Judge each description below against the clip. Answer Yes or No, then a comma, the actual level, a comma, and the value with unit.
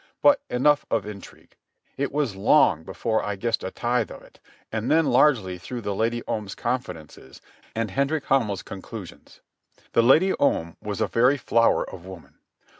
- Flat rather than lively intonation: No, wide, 5.6 semitones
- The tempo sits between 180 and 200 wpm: No, average, 165 wpm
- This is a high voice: No, low, 115 Hz